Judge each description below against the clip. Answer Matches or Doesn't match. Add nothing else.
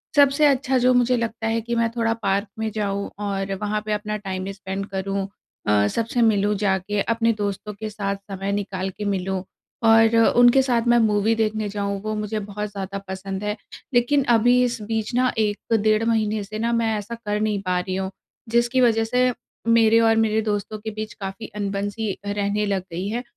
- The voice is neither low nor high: Doesn't match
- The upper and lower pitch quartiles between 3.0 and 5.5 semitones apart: Doesn't match